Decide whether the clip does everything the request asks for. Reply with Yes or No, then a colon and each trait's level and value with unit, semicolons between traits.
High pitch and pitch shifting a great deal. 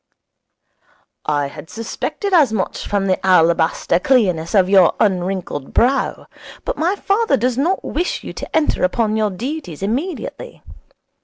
Yes: high, 215 Hz; wide, 8.2 semitones